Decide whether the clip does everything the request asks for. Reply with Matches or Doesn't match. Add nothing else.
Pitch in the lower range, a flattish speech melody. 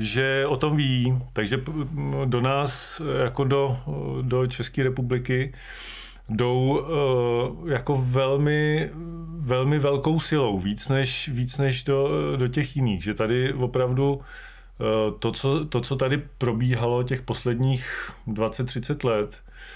Matches